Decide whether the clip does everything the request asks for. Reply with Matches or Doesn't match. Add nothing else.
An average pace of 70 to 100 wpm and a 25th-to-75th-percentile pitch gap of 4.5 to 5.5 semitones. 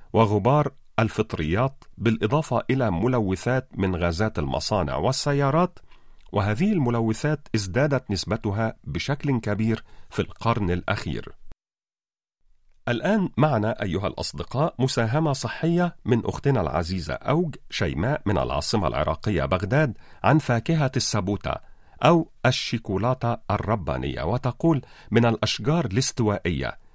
Matches